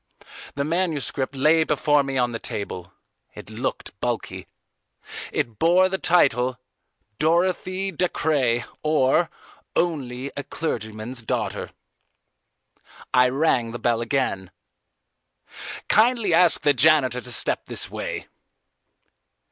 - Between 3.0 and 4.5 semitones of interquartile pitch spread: No, average, 5.1 semitones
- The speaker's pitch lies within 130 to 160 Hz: Yes, medium, 140 Hz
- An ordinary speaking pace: No, slow, 110 wpm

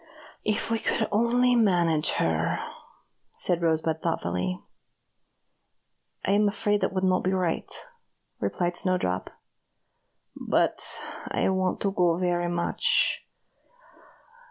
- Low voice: No, medium, 180 Hz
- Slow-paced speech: Yes, slow, 110 wpm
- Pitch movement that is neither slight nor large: Yes, average, 3.6 semitones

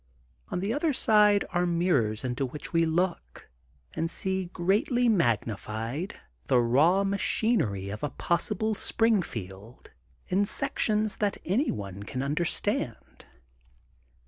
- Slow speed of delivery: Yes, slow, 120 wpm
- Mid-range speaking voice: Yes, medium, 175 Hz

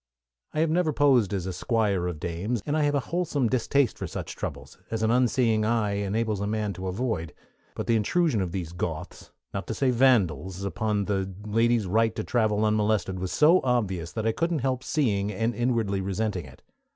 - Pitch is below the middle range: Yes, low, 110 Hz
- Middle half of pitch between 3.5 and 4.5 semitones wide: Yes, average, 4.2 semitones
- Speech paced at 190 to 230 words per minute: Yes, average, 200 wpm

